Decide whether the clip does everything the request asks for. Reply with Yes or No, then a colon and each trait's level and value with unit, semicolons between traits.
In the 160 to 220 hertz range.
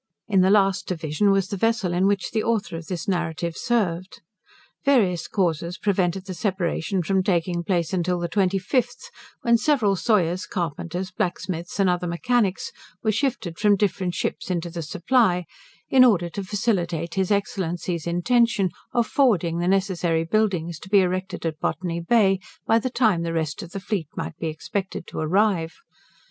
Yes: medium, 185 Hz